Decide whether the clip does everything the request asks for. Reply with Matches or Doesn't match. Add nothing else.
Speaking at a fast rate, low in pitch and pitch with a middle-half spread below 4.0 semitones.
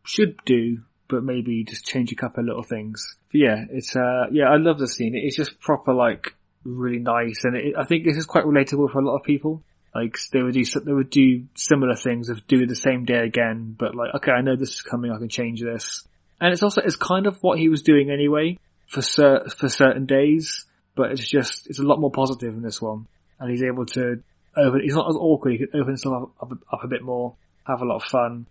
Matches